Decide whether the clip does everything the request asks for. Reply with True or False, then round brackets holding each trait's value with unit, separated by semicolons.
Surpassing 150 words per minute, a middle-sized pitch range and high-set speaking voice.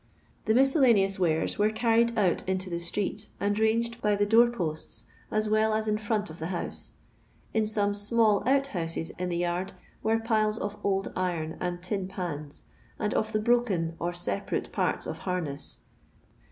True (175 wpm; 3.7 semitones; 205 Hz)